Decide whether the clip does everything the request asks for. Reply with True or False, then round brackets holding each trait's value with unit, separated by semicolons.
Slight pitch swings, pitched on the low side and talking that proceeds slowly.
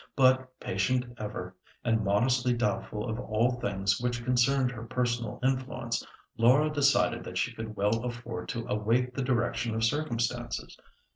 False (2.1 semitones; 120 Hz; 145 wpm)